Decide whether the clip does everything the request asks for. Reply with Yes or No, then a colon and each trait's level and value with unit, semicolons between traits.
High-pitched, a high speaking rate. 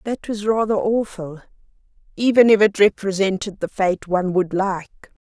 No: high, 200 Hz; average, 145 wpm